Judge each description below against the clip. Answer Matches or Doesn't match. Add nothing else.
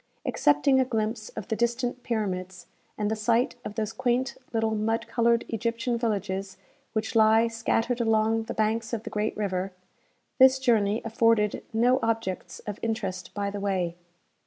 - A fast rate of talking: Doesn't match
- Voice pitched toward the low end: Doesn't match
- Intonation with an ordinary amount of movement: Doesn't match